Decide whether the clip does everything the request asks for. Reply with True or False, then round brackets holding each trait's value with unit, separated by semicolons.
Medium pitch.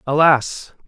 True (145 Hz)